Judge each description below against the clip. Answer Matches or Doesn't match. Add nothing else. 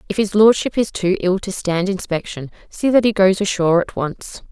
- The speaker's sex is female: Matches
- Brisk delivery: Matches